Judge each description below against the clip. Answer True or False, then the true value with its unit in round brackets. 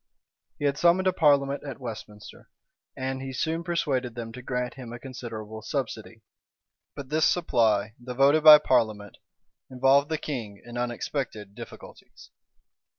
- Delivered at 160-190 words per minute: False (145 wpm)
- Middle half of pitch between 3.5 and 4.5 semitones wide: True (4.0 semitones)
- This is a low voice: True (130 Hz)